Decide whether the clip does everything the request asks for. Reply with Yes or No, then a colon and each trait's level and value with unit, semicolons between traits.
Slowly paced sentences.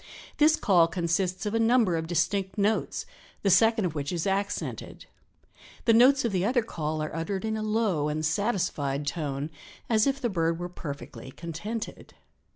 No: average, 170 wpm